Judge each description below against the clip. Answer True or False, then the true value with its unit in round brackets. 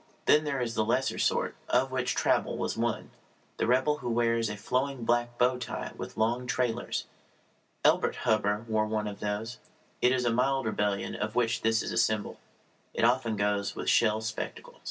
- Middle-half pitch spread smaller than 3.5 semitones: True (2.5 semitones)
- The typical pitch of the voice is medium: False (115 Hz)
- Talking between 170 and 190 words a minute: True (180 wpm)